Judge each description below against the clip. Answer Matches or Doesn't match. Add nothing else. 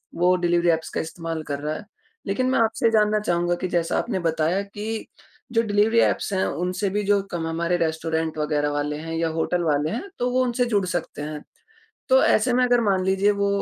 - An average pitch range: Matches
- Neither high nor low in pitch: Matches